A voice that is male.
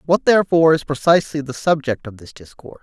Yes: male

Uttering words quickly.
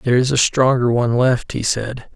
Yes: fast, 220 wpm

